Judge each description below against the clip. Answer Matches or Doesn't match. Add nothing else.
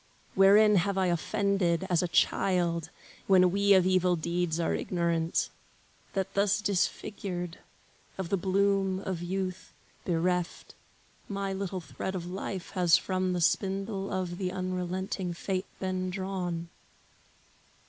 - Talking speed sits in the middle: Doesn't match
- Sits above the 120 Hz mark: Matches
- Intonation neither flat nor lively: Doesn't match